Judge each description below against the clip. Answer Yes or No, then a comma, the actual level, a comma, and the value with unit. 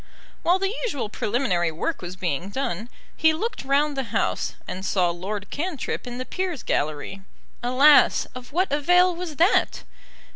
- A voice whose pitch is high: Yes, very high, 265 Hz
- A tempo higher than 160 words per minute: No, average, 155 wpm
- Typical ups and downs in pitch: No, wide, 9.0 semitones